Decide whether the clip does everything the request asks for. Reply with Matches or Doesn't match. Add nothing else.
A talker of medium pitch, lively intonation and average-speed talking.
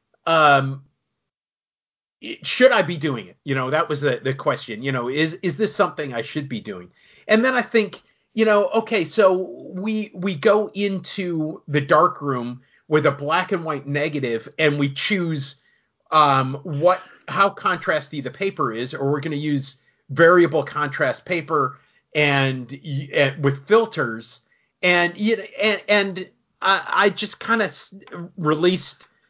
Matches